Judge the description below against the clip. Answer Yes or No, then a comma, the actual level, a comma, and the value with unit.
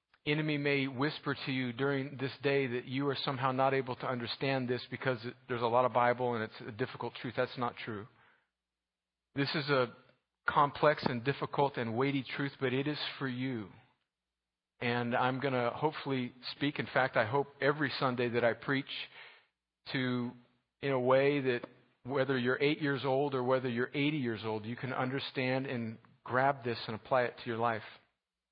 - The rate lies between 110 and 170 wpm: No, average, 185 wpm